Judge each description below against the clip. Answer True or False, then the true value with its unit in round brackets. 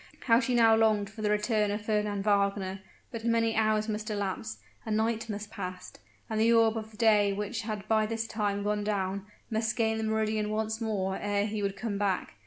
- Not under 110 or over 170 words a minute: False (200 wpm)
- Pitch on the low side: False (215 Hz)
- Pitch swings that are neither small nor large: False (1.4 semitones)